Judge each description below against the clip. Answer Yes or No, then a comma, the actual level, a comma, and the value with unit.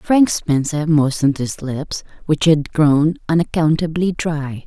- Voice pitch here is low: No, medium, 155 Hz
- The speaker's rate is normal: No, slow, 130 wpm